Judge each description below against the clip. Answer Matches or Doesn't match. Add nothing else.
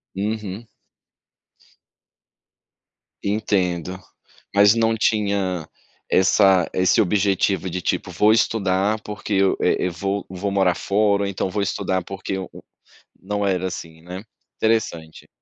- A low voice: Matches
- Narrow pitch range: Matches